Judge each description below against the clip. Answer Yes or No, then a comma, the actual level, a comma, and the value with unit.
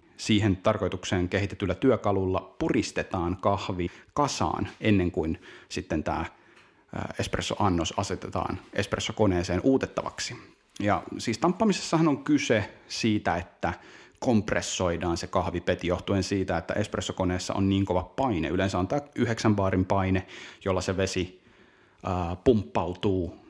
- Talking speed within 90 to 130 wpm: Yes, average, 110 wpm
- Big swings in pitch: No, average, 3.1 semitones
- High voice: No, very low, 95 Hz